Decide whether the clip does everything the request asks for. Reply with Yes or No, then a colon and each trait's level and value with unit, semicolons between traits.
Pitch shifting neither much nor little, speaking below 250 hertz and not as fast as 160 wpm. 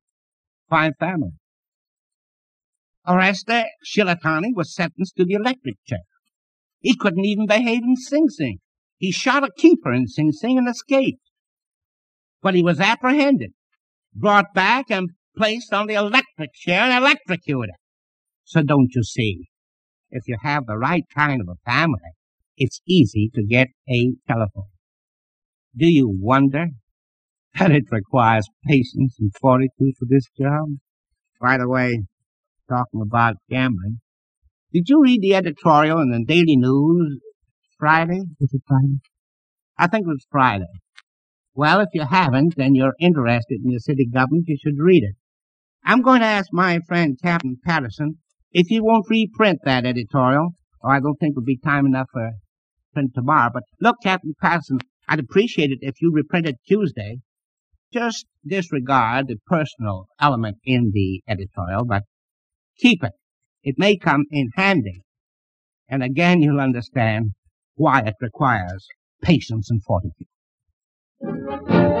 No: wide, 7.2 semitones; medium, 140 Hz; average, 145 wpm